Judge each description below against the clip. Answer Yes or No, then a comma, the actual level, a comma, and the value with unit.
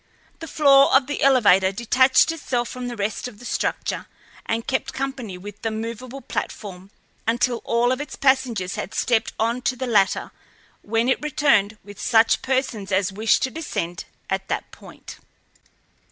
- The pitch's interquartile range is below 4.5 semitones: Yes, average, 4.1 semitones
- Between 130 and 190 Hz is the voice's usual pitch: No, high, 235 Hz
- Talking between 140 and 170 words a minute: Yes, average, 165 wpm